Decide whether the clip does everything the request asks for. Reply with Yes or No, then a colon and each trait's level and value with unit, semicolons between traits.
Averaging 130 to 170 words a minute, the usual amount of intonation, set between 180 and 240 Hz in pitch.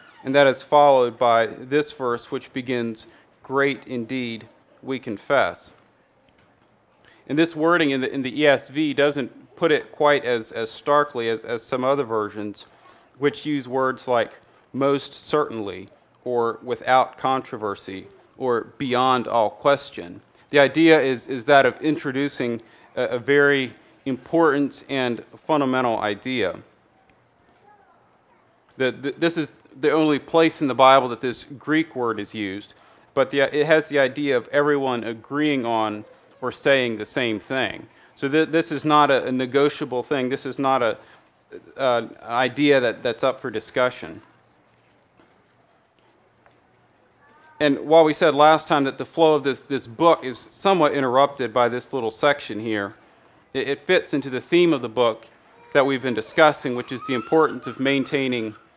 No: average, 155 wpm; average, 3.1 semitones; low, 135 Hz